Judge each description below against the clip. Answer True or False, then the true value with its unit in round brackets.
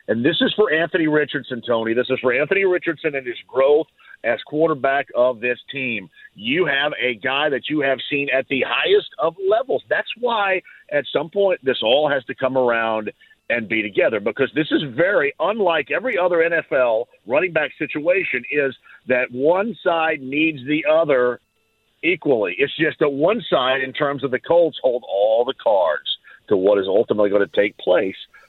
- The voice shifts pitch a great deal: True (7.3 semitones)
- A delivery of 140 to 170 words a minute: False (185 wpm)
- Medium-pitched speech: True (150 Hz)